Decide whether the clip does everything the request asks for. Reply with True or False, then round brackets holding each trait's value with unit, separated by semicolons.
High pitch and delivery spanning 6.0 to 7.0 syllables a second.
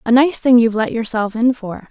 True (235 Hz; 6.1 syllables/s)